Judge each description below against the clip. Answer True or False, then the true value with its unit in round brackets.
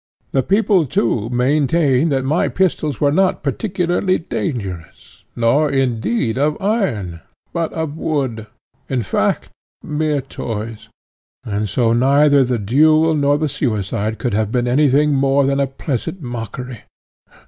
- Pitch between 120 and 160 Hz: True (135 Hz)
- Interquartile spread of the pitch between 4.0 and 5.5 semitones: True (4.8 semitones)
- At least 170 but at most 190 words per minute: False (135 wpm)